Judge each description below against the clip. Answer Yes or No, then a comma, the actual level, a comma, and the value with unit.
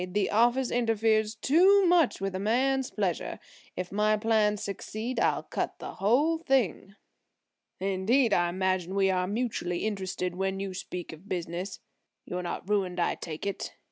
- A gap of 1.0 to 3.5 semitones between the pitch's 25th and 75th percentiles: No, average, 4.0 semitones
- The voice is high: Yes, high, 200 Hz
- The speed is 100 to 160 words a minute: Yes, average, 155 wpm